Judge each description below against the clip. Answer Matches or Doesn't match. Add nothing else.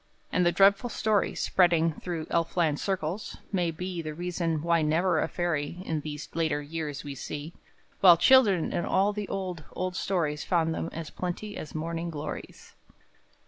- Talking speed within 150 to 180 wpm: Matches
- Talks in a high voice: Doesn't match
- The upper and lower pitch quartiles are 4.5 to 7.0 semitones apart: Doesn't match